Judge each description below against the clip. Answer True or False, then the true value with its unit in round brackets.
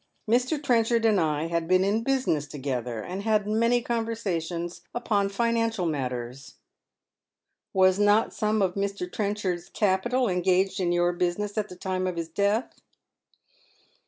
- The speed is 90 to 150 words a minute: True (145 wpm)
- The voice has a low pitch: False (195 Hz)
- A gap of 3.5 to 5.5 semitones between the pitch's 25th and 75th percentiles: True (4.2 semitones)